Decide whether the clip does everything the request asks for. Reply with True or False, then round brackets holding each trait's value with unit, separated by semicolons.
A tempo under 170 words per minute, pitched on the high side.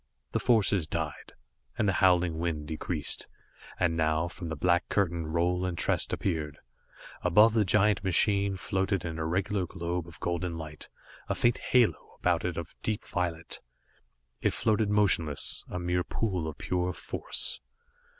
False (150 wpm; 90 Hz)